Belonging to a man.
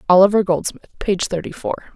No: female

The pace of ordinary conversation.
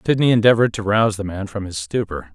No: fast, 230 wpm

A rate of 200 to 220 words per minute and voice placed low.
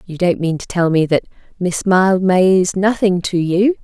No: fast, 205 wpm; medium, 185 Hz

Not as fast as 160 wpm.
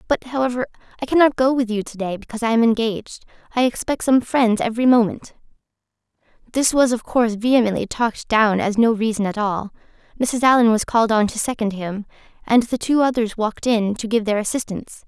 No: average, 190 wpm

